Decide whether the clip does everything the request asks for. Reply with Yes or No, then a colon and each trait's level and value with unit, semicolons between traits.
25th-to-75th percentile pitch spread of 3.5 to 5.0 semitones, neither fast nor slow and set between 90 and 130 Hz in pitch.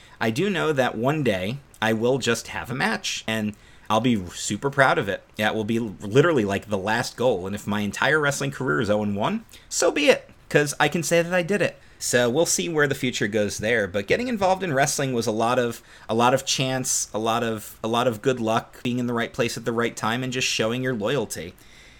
No: average, 3.8 semitones; fast, 245 wpm; low, 120 Hz